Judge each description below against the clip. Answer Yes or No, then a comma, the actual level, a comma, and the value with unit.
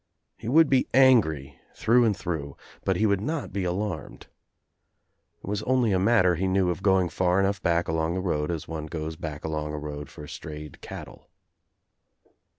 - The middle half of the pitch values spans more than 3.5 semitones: Yes, average, 4.8 semitones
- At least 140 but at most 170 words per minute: No, average, 180 wpm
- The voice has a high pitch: No, very low, 90 Hz